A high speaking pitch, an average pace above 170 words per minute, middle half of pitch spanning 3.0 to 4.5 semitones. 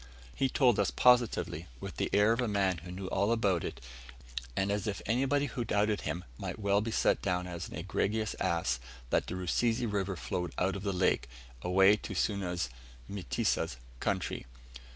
No: low, 100 Hz; average, 180 wpm; average, 3.4 semitones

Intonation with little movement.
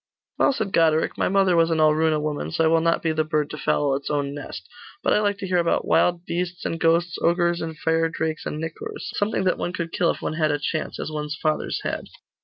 Yes: narrow, 2.0 semitones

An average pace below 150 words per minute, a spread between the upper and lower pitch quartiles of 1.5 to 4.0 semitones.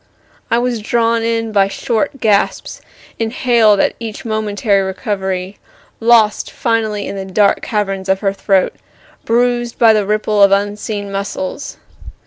Yes: slow, 135 wpm; narrow, 2.5 semitones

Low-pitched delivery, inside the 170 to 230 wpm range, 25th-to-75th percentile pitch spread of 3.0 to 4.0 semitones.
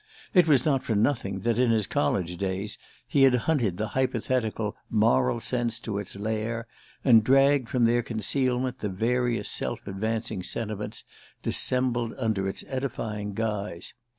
No: low, 115 Hz; average, 150 wpm; average, 3.3 semitones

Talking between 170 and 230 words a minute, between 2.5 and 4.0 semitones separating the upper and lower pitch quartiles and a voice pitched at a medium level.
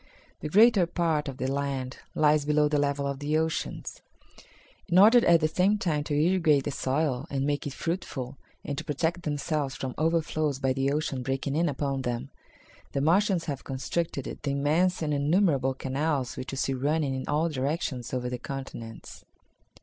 Yes: average, 180 wpm; average, 3.1 semitones; medium, 145 Hz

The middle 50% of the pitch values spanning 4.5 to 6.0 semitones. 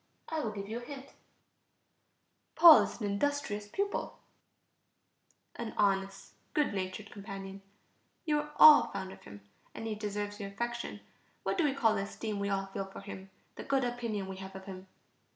No: average, 3.8 semitones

